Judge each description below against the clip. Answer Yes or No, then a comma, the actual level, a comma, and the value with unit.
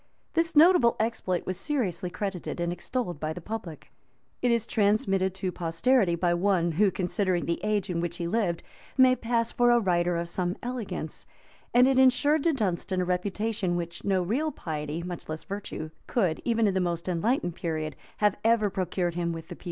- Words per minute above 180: Yes, average, 190 wpm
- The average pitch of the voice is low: No, medium, 185 Hz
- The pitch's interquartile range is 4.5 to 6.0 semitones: Yes, average, 4.9 semitones